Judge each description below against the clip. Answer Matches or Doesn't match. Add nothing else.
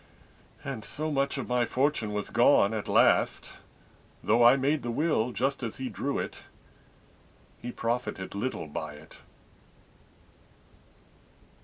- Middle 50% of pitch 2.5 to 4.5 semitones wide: Matches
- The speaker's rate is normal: Doesn't match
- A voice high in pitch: Doesn't match